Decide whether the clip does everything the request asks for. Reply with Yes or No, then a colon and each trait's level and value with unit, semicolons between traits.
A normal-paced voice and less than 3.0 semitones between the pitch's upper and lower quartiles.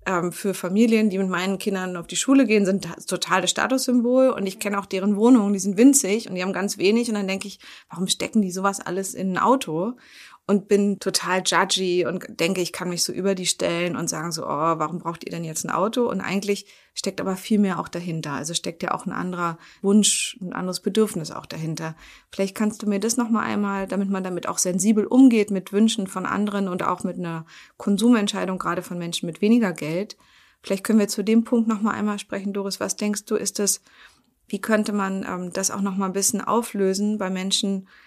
No: fast, 220 wpm; narrow, 2.5 semitones